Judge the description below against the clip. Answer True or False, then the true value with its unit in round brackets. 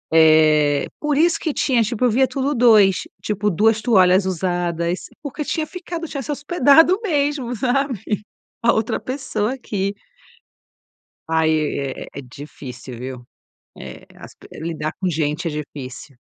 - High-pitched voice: True (210 Hz)